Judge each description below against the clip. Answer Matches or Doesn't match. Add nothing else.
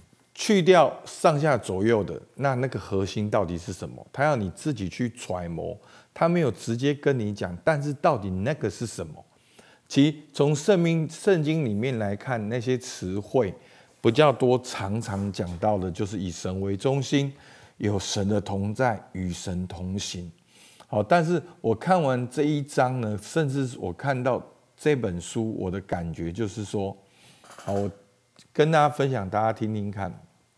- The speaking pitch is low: Matches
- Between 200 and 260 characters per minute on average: Matches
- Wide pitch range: Matches